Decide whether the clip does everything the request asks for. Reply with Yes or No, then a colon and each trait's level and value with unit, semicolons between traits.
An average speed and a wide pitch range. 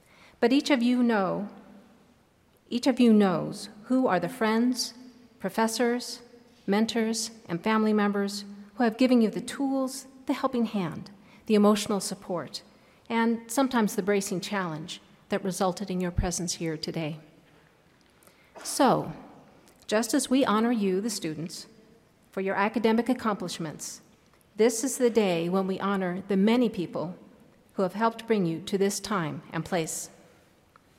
No: average, 145 wpm; average, 4.0 semitones